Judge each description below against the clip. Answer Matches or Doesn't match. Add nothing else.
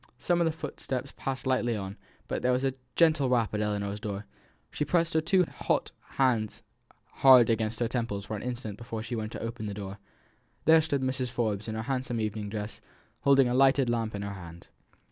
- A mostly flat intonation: Doesn't match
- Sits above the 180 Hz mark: Doesn't match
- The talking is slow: Doesn't match